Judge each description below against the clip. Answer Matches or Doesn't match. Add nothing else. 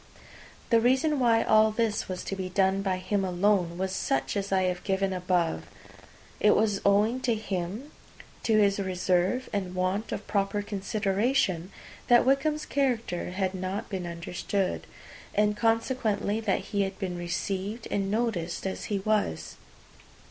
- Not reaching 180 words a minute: Matches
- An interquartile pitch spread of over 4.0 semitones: Doesn't match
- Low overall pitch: Doesn't match